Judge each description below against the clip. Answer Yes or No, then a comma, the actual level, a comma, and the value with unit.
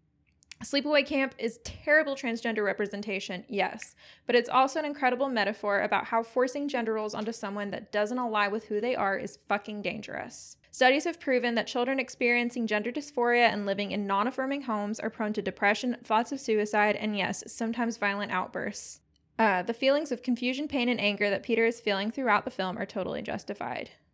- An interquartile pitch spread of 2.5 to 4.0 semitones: Yes, average, 3.6 semitones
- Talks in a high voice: Yes, high, 225 Hz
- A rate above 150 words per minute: Yes, average, 185 wpm